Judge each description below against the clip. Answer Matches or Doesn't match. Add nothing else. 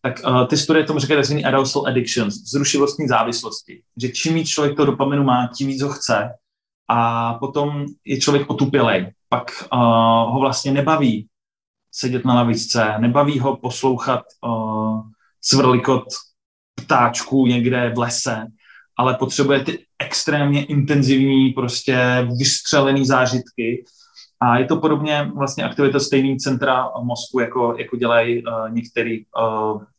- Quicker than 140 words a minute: Doesn't match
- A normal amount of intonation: Matches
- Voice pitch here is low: Matches